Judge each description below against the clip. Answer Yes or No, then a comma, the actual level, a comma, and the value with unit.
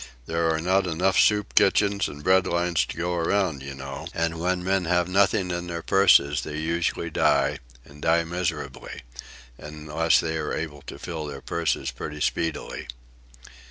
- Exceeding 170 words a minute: No, average, 160 wpm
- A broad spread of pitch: No, average, 3.0 semitones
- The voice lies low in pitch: Yes, very low, 85 Hz